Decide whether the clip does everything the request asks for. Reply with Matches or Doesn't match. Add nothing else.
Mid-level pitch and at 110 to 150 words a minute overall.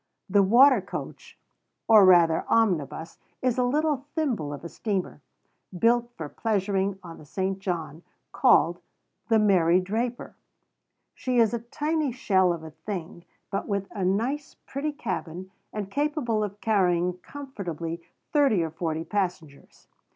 Doesn't match